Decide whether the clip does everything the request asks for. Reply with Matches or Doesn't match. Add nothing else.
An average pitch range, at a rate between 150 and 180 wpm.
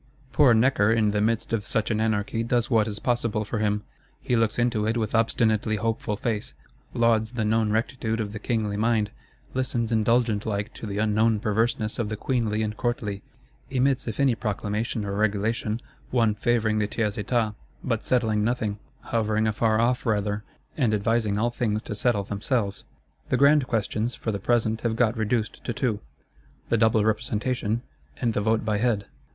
Doesn't match